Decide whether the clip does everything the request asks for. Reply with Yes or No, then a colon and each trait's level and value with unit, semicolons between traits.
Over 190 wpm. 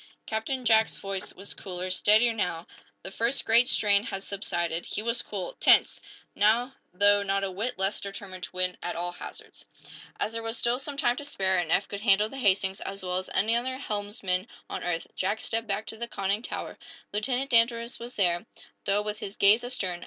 Yes: average, 200 wpm